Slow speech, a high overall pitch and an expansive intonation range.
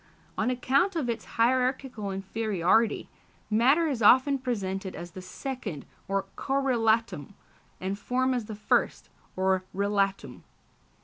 No: slow, 120 wpm; high, 225 Hz; average, 4.8 semitones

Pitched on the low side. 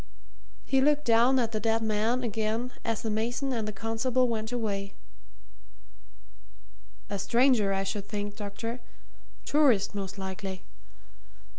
No: high, 225 Hz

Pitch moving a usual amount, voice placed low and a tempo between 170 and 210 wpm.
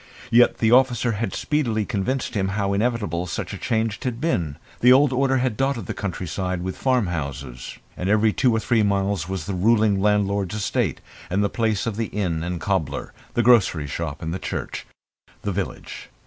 Yes: average, 4.2 semitones; low, 105 Hz; average, 180 wpm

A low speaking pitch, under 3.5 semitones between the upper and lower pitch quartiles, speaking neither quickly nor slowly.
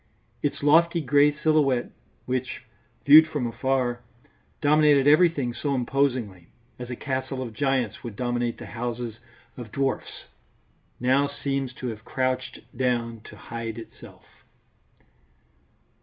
No: low, 130 Hz; average, 2.9 semitones; slow, 120 wpm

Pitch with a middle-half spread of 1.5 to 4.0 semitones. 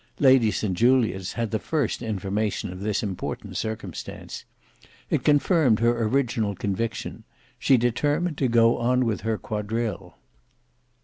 Yes: average, 3.2 semitones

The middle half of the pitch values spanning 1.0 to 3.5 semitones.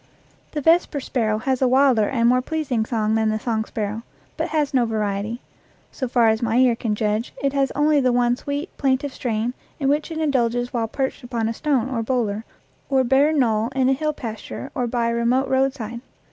Yes: average, 3.2 semitones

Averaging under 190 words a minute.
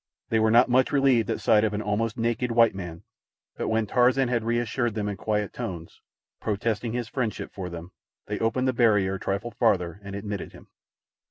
No: average, 195 wpm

